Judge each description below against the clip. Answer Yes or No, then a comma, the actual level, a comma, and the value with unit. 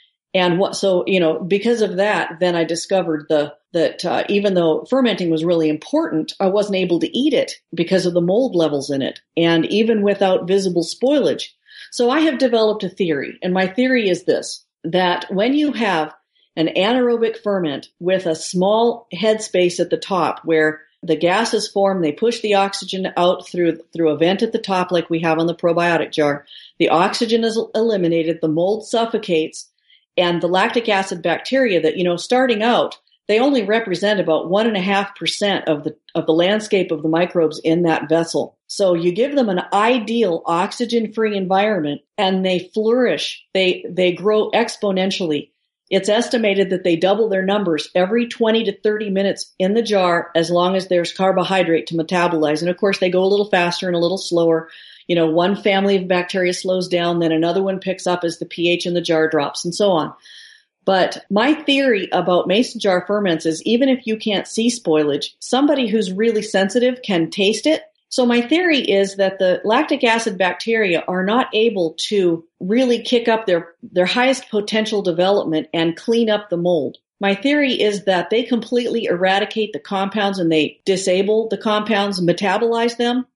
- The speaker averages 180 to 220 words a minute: Yes, average, 185 wpm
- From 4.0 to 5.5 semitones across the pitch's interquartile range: Yes, average, 4.5 semitones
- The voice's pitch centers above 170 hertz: Yes, high, 190 Hz